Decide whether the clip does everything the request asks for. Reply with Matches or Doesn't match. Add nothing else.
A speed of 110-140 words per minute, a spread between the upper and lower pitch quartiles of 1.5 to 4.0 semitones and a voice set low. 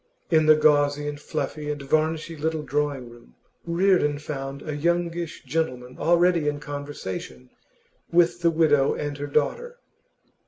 Doesn't match